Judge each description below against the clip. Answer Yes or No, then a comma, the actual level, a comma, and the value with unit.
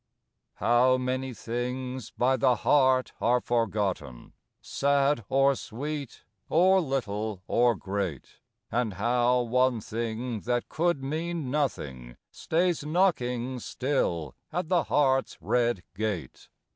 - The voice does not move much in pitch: No, average, 3.5 semitones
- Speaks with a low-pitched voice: Yes, low, 125 Hz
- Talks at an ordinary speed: No, slow, 115 wpm